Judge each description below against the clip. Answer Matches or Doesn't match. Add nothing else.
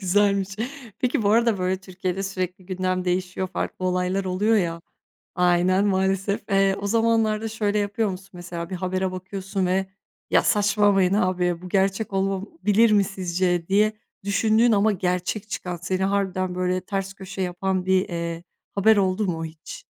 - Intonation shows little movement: Matches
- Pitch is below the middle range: Doesn't match